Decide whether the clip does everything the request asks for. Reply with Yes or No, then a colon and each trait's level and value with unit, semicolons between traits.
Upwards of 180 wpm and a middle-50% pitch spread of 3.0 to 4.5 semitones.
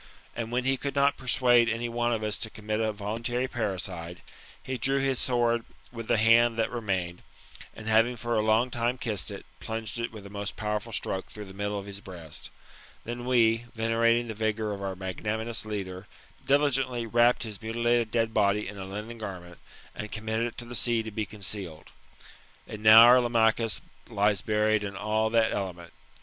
No: average, 190 wpm; narrow, 2.4 semitones